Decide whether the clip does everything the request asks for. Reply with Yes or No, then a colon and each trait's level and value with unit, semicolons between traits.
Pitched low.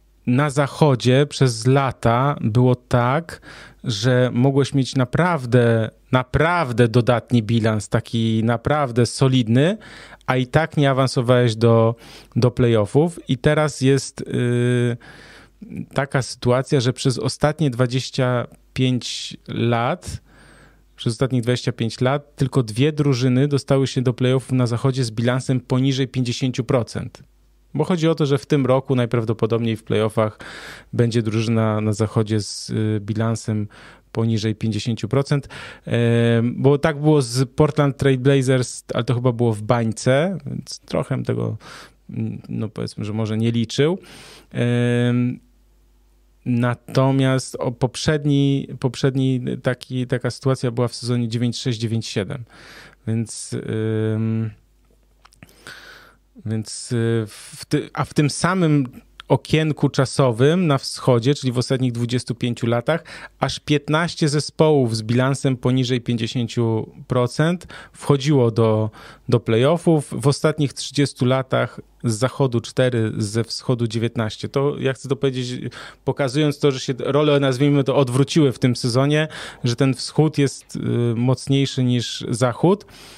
Yes: low, 130 Hz